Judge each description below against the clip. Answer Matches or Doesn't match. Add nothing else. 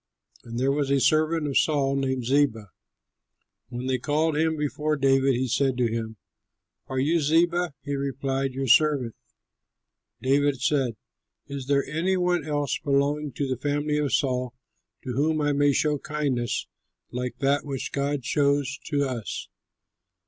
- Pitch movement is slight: Matches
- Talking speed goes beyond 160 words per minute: Doesn't match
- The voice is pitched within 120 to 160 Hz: Matches